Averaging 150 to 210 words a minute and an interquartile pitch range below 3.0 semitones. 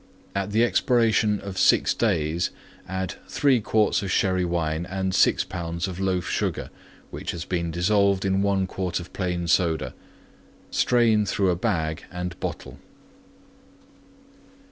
No: average, 140 wpm; narrow, 2.5 semitones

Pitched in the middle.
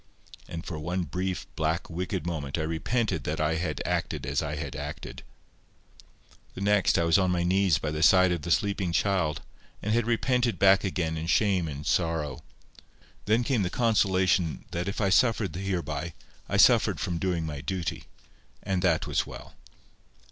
No: very low, 90 Hz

